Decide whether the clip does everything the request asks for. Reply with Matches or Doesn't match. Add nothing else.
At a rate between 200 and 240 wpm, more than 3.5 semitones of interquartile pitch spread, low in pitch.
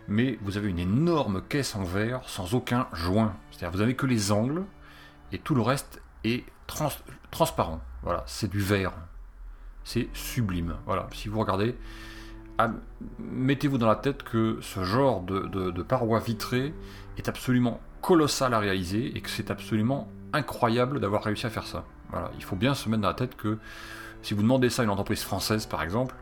Doesn't match